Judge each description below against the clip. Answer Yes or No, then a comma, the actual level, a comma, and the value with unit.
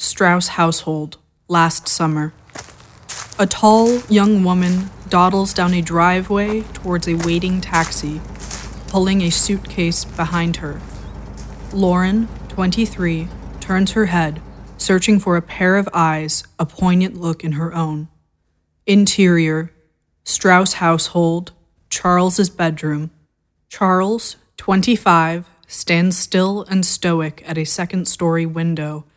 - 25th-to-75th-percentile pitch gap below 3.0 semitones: Yes, narrow, 2.5 semitones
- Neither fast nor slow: No, slow, 110 wpm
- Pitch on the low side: No, medium, 175 Hz